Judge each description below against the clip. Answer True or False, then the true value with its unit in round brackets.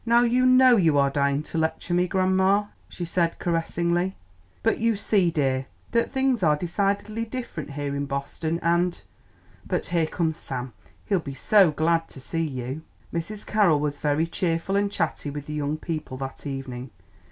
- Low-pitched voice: False (165 Hz)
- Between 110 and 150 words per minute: False (175 wpm)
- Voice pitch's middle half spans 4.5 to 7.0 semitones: True (5.3 semitones)